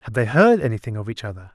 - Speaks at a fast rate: Yes, fast, 270 wpm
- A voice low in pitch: Yes, low, 125 Hz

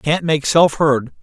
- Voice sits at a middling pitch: Yes, medium, 150 Hz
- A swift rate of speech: No, average, 195 wpm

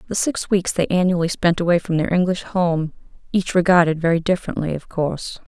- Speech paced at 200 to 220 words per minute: No, average, 185 wpm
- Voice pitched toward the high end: No, medium, 175 Hz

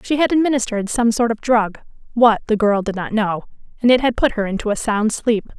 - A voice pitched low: No, high, 225 Hz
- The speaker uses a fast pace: Yes, fast, 215 wpm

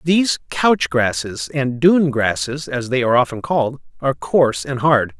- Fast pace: No, average, 175 wpm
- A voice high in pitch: No, low, 130 Hz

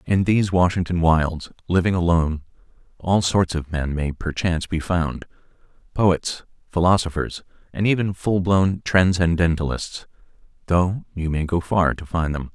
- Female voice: No, male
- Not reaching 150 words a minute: Yes, slow, 135 wpm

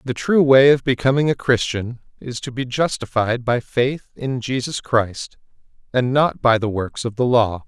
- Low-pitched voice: Yes, low, 125 Hz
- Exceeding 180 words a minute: Yes, average, 190 wpm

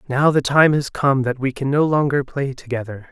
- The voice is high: No, low, 135 Hz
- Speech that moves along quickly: Yes, fast, 230 wpm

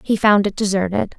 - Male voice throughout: No, female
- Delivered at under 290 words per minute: Yes, fast, 205 wpm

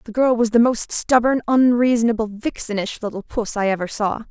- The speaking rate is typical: Yes, average, 180 wpm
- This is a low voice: No, high, 225 Hz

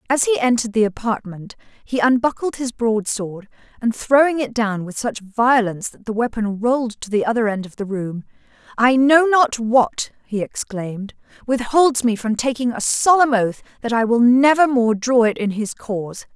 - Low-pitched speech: No, high, 230 Hz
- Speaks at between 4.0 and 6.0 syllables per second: Yes, 4.9 syllables/s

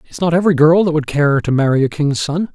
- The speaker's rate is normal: No, fast, 280 wpm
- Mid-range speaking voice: Yes, medium, 155 Hz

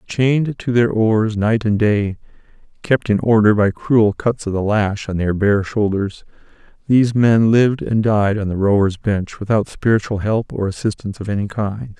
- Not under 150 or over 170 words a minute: No, average, 185 wpm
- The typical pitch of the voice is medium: No, low, 110 Hz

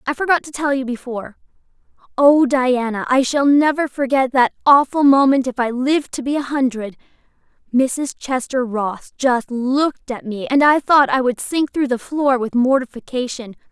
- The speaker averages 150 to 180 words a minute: Yes, average, 175 wpm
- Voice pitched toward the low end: No, very high, 260 Hz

